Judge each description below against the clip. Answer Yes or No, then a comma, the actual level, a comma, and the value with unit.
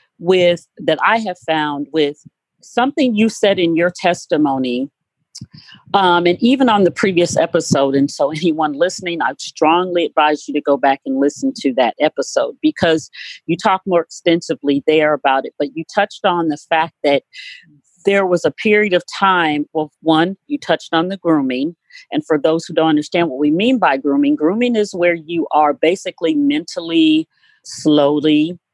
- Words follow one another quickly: No, average, 170 wpm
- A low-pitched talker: No, medium, 165 Hz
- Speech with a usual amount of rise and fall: Yes, average, 4.4 semitones